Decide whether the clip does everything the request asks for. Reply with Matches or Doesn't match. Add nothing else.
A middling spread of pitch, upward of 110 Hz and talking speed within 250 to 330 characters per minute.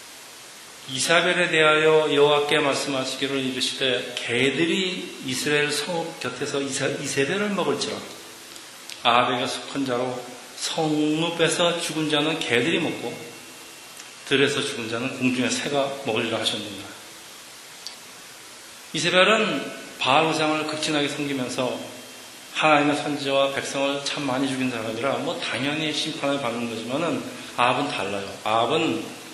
Matches